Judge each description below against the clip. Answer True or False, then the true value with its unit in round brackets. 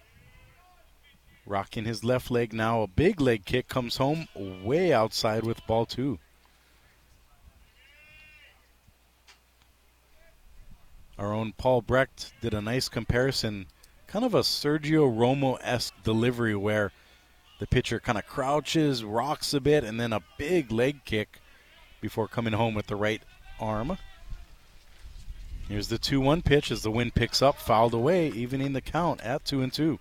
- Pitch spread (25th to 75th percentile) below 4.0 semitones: False (4.4 semitones)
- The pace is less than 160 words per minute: True (140 wpm)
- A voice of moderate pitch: False (115 Hz)